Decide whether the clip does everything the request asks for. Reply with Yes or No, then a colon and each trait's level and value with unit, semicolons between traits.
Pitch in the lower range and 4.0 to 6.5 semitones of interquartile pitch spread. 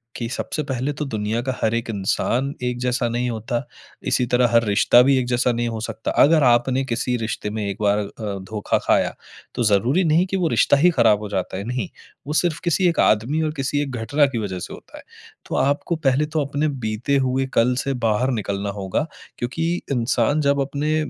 Yes: low, 125 Hz; average, 4.3 semitones